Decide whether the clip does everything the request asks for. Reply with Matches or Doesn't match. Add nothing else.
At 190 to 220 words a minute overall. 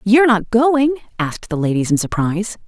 Matches